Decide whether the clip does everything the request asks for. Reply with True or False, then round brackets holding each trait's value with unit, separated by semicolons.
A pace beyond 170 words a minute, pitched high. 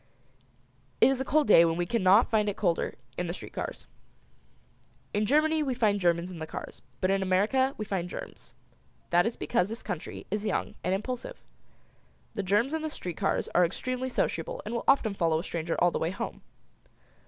True (200 wpm; 205 Hz)